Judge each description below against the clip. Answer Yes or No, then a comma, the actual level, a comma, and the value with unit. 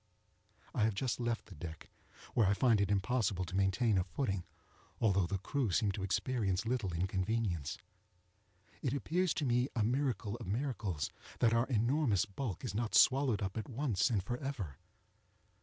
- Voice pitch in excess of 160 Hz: No, low, 110 Hz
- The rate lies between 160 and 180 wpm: Yes, average, 165 wpm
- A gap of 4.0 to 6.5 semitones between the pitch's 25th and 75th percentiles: Yes, average, 4.4 semitones